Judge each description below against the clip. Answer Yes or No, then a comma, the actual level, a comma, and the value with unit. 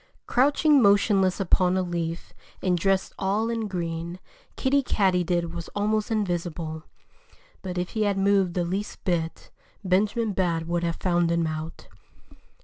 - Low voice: No, medium, 185 Hz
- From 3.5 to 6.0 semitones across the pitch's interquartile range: No, average, 3.1 semitones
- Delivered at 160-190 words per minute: No, average, 140 wpm